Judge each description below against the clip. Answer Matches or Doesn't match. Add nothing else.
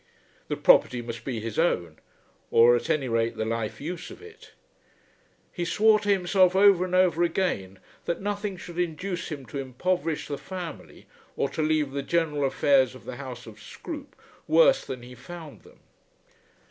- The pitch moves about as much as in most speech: Doesn't match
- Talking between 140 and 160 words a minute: Doesn't match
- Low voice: Doesn't match